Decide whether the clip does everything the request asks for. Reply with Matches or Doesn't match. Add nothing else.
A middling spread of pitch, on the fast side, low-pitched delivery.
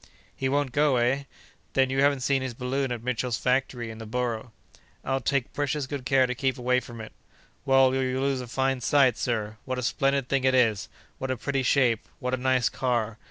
Doesn't match